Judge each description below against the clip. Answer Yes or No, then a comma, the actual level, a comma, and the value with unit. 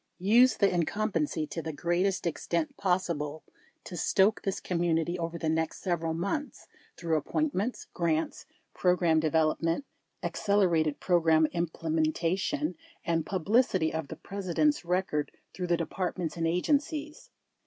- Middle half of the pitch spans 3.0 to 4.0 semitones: Yes, average, 3.4 semitones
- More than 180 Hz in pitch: No, medium, 175 Hz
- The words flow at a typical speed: No, slow, 130 wpm